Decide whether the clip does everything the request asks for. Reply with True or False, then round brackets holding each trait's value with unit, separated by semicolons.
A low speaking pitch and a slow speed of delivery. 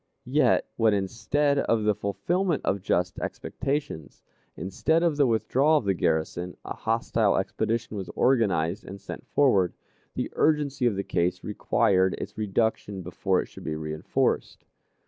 False (105 Hz; 145 wpm)